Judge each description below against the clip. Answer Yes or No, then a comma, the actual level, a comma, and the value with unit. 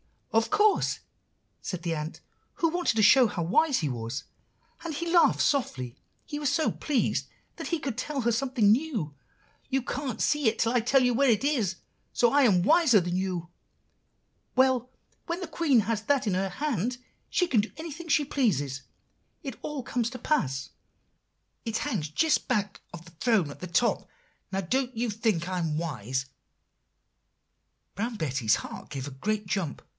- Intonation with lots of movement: Yes, wide, 8.0 semitones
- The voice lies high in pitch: Yes, high, 225 Hz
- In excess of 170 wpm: Yes, average, 180 wpm